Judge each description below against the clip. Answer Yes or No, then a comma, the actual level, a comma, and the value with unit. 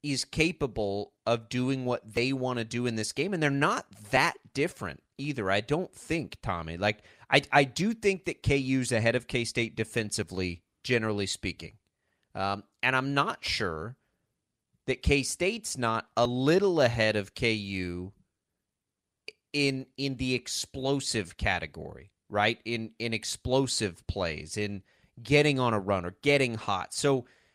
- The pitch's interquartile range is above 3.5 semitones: Yes, average, 4.9 semitones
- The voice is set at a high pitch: No, low, 120 Hz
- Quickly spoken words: No, average, 150 wpm